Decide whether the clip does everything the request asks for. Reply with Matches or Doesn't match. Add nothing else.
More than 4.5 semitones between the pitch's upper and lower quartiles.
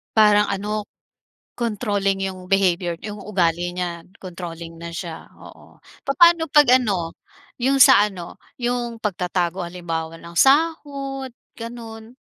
Matches